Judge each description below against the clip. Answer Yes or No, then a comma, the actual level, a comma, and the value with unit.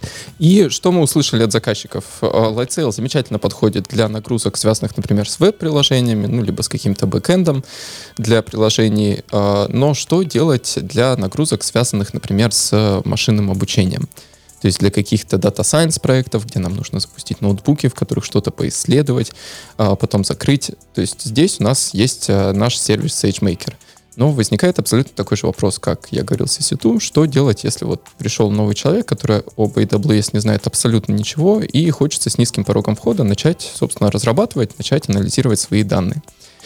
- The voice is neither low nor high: No, low, 115 Hz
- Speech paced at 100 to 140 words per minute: No, average, 155 wpm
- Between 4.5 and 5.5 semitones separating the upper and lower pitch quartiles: Yes, average, 5.1 semitones